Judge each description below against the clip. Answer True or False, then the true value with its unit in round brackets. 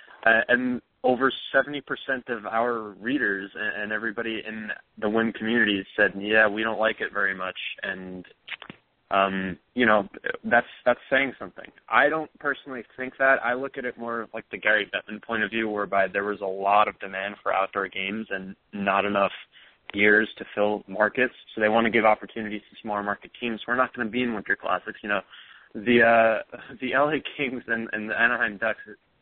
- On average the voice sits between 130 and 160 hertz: False (110 Hz)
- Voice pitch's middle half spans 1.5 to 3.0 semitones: True (2.7 semitones)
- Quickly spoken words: False (190 wpm)